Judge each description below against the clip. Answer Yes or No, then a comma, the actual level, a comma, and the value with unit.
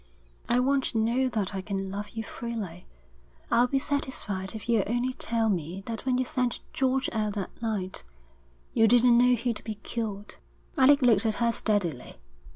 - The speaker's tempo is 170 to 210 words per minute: Yes, average, 175 wpm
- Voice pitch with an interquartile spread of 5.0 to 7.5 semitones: No, average, 3.4 semitones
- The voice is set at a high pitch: Yes, high, 230 Hz